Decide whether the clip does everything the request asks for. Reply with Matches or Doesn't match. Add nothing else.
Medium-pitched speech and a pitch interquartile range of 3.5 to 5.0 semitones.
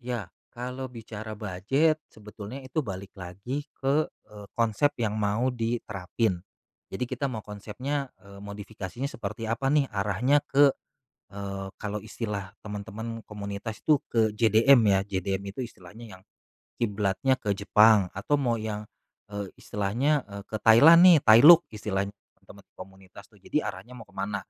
Doesn't match